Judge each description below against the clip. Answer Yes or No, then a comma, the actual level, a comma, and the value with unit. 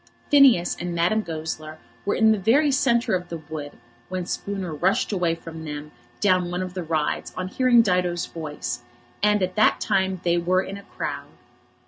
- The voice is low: No, medium, 180 Hz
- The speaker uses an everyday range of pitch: Yes, average, 3.6 semitones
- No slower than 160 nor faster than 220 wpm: Yes, average, 180 wpm